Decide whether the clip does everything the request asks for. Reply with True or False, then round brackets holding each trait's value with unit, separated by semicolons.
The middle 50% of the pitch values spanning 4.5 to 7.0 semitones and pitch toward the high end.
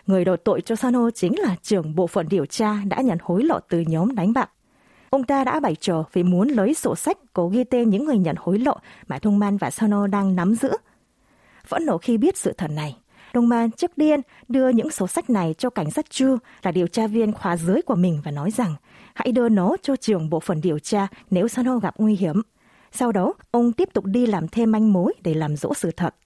True (5.2 semitones; 210 Hz)